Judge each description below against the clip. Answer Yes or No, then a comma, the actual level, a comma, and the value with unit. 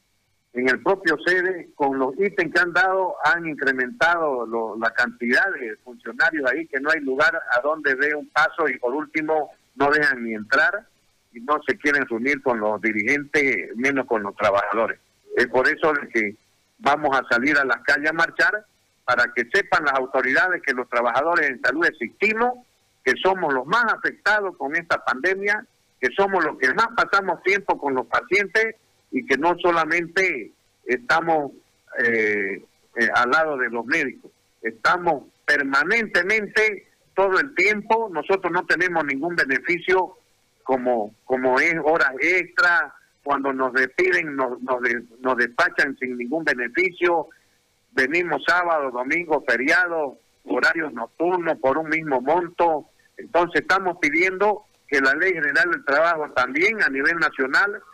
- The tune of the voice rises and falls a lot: Yes, wide, 6.6 semitones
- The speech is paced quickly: No, average, 155 wpm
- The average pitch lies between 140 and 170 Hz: Yes, medium, 155 Hz